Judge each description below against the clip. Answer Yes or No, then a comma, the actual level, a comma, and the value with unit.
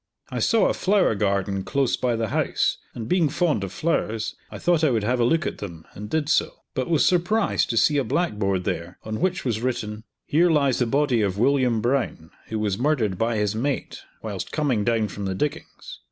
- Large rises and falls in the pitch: Yes, wide, 6.3 semitones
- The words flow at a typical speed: No, fast, 210 wpm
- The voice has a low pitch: Yes, low, 120 Hz